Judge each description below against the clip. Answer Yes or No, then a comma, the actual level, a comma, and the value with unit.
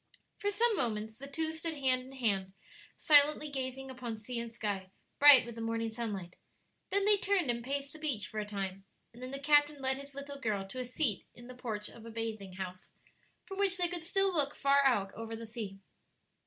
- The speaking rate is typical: No, fast, 215 wpm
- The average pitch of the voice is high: Yes, very high, 255 Hz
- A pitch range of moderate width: Yes, average, 4.8 semitones